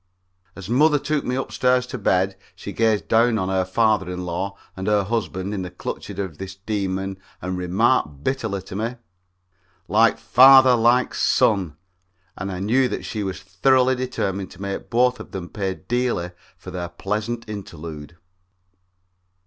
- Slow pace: No, average, 160 wpm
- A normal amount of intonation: Yes, average, 4.4 semitones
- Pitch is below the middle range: Yes, low, 100 Hz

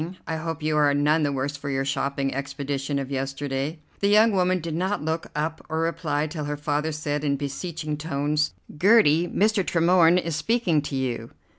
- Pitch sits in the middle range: Yes, medium, 150 Hz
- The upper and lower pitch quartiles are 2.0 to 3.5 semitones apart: Yes, average, 2.8 semitones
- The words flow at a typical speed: Yes, average, 185 wpm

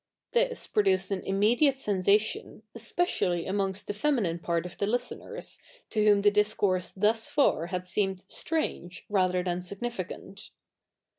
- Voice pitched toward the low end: No, high, 200 Hz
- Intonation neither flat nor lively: Yes, average, 3.0 semitones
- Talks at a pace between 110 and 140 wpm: Yes, slow, 135 wpm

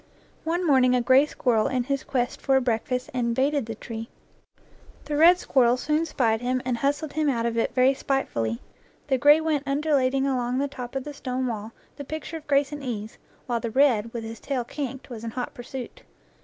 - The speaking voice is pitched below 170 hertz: No, very high, 260 Hz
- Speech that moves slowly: No, fast, 205 wpm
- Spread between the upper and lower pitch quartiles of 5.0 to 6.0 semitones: No, average, 3.0 semitones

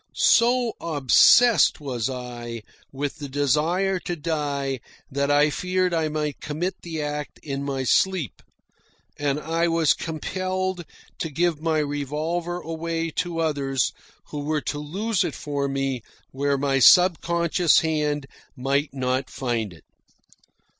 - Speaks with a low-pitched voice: No, medium, 150 Hz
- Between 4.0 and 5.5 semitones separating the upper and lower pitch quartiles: No, average, 3.5 semitones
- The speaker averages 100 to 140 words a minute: Yes, slow, 135 wpm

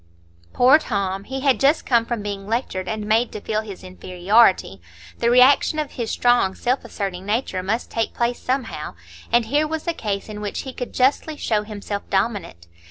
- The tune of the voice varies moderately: Yes, average, 4.0 semitones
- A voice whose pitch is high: Yes, high, 225 Hz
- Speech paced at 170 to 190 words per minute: Yes, average, 185 wpm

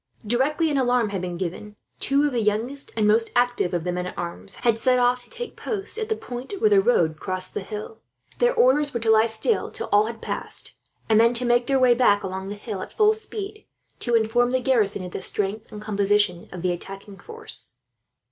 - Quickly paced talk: Yes, fast, 225 wpm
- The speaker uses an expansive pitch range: No, average, 4.7 semitones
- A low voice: No, high, 230 Hz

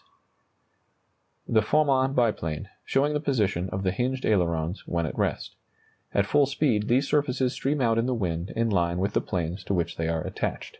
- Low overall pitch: Yes, low, 110 Hz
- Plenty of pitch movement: Yes, wide, 7.1 semitones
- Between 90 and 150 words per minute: No, average, 190 wpm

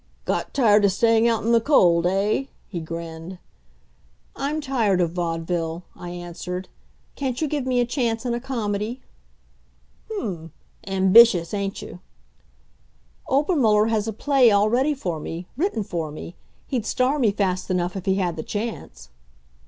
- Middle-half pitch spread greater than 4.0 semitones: Yes, wide, 5.5 semitones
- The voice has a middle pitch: No, high, 205 Hz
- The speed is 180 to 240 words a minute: No, average, 155 wpm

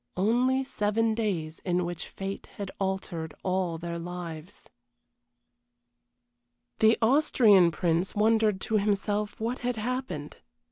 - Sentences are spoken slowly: Yes, slow, 110 wpm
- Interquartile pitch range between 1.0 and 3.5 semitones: No, average, 4.2 semitones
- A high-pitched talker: Yes, high, 200 Hz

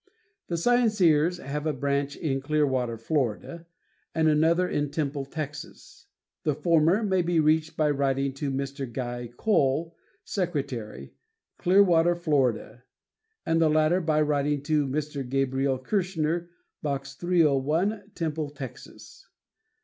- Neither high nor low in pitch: Yes, medium, 150 Hz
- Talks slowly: Yes, slow, 120 wpm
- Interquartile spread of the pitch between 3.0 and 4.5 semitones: Yes, average, 3.4 semitones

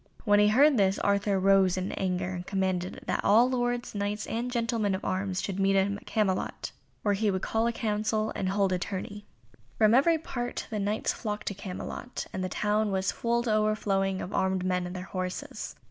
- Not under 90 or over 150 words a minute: No, fast, 205 wpm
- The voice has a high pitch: Yes, high, 200 Hz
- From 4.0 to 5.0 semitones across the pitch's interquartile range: No, narrow, 2.4 semitones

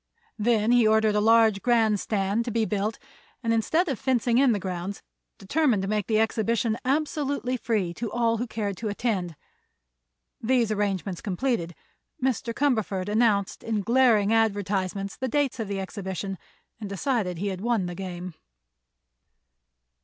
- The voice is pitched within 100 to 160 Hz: No, high, 220 Hz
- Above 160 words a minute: No, average, 155 wpm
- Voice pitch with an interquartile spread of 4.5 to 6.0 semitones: No, average, 3.3 semitones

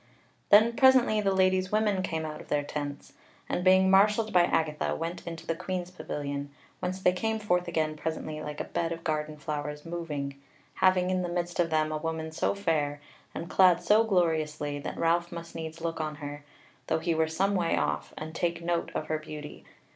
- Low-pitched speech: No, medium, 165 Hz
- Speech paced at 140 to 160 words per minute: No, average, 200 wpm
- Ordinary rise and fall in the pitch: Yes, average, 3.1 semitones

